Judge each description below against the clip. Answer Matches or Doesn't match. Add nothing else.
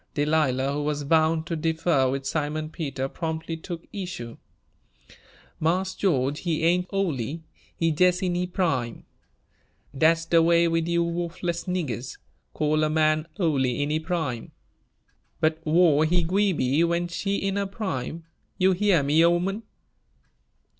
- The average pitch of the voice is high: Doesn't match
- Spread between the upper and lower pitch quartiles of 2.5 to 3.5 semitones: Matches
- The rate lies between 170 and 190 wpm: Doesn't match